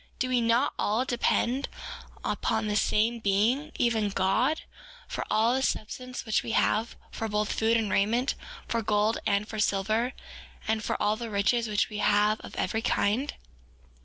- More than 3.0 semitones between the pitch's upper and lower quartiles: No, narrow, 2.4 semitones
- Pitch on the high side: Yes, high, 220 Hz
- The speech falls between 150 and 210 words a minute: Yes, average, 170 wpm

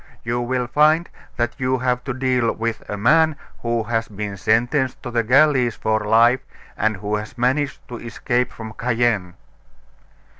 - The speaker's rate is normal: Yes, average, 160 wpm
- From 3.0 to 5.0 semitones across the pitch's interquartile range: No, narrow, 2.5 semitones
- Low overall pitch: Yes, low, 120 Hz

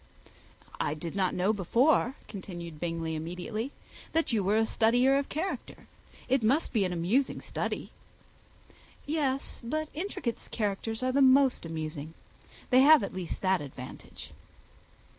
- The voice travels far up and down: Yes, wide, 7.4 semitones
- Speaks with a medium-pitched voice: No, high, 220 Hz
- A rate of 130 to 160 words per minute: Yes, average, 140 wpm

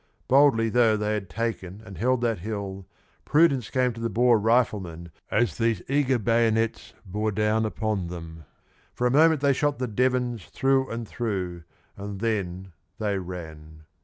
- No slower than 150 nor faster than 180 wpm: Yes, average, 160 wpm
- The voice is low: Yes, low, 110 Hz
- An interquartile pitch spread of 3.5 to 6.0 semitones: Yes, average, 4.2 semitones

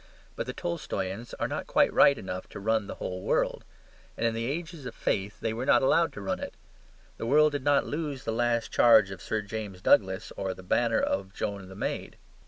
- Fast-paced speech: Yes, fast, 215 wpm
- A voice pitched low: Yes, low, 115 Hz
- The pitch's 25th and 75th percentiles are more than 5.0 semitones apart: Yes, wide, 5.4 semitones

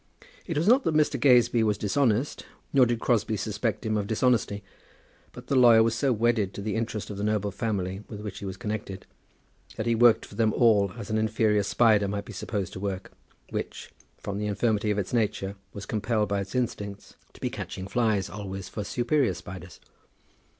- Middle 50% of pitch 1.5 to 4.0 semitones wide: Yes, average, 2.7 semitones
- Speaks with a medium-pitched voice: No, low, 110 Hz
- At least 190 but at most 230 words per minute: Yes, average, 200 wpm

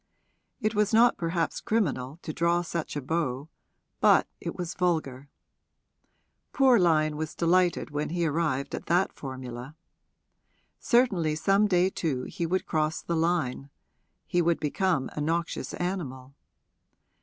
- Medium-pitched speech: Yes, medium, 165 Hz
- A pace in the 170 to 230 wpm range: No, slow, 135 wpm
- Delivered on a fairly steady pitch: No, average, 3.4 semitones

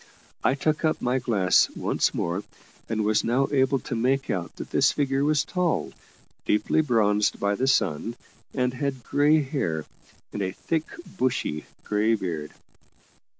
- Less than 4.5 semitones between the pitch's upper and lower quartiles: No, average, 5.3 semitones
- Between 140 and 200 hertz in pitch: No, low, 125 Hz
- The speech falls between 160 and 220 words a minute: No, average, 150 wpm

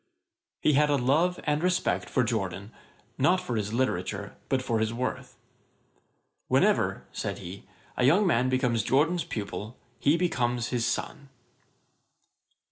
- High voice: No, low, 130 Hz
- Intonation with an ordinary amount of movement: Yes, average, 4.6 semitones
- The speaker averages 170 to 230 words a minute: No, average, 140 wpm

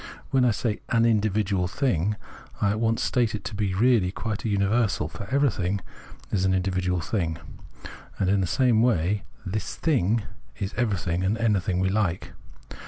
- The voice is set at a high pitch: No, low, 100 Hz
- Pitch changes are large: No, average, 3.5 semitones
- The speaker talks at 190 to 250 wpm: No, average, 175 wpm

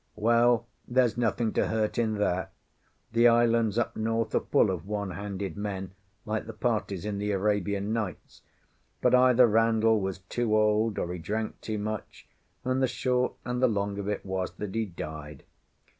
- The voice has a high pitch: No, low, 110 Hz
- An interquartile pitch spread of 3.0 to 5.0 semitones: No, narrow, 2.6 semitones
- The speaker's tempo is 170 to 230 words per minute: Yes, average, 180 wpm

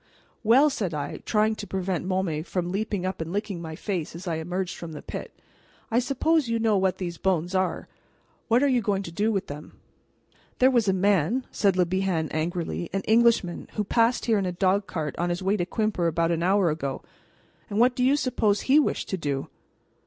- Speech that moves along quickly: Yes, fast, 210 wpm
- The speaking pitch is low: No, high, 190 Hz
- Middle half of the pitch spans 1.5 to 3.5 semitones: No, average, 4.2 semitones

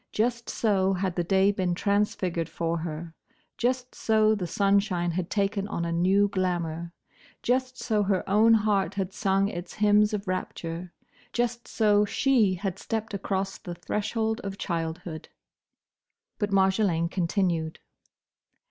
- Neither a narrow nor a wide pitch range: Yes, average, 3.2 semitones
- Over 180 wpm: No, average, 140 wpm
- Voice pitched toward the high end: Yes, high, 195 Hz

